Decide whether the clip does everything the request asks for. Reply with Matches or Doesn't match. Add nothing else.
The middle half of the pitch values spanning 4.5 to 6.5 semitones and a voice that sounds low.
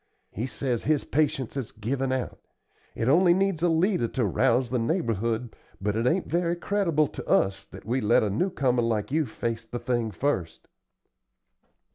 Matches